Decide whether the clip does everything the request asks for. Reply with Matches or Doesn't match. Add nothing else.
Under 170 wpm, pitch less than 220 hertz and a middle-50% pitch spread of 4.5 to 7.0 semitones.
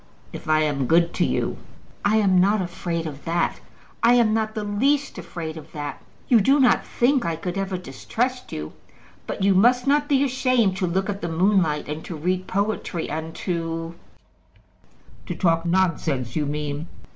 Doesn't match